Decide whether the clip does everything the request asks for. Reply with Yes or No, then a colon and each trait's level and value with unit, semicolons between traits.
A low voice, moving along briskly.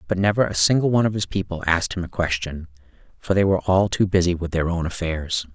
Yes: very low, 90 Hz; fast, 240 wpm